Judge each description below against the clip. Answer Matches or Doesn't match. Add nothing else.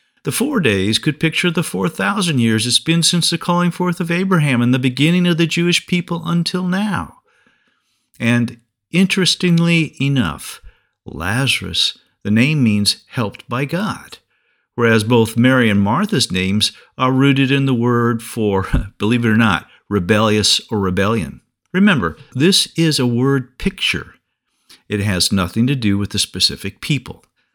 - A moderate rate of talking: Matches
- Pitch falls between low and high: Doesn't match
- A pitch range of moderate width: Doesn't match